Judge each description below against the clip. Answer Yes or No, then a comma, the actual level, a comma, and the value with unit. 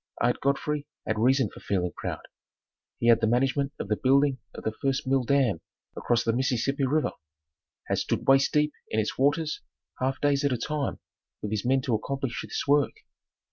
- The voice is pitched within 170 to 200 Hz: No, low, 135 Hz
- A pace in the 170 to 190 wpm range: Yes, average, 185 wpm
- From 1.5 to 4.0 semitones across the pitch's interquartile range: Yes, average, 3.0 semitones